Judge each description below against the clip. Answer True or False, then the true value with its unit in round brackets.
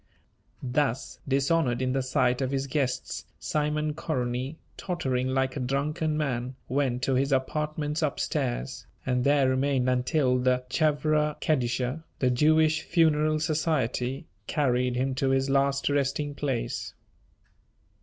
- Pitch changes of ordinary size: True (3.0 semitones)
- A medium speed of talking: False (130 wpm)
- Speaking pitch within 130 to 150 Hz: True (135 Hz)